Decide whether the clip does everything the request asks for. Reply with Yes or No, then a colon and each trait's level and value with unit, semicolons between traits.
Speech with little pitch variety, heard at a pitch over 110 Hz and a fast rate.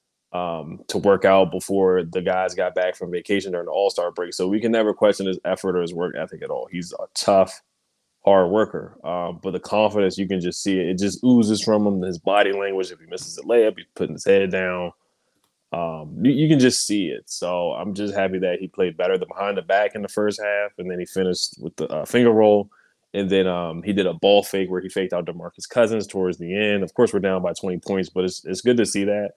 No: narrow, 2.1 semitones; very low, 95 Hz; fast, 250 wpm